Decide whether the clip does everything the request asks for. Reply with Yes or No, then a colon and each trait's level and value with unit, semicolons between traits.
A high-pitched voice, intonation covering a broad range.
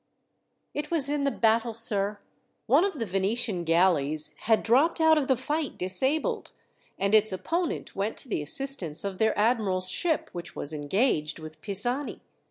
Yes: high, 220 Hz; wide, 6.8 semitones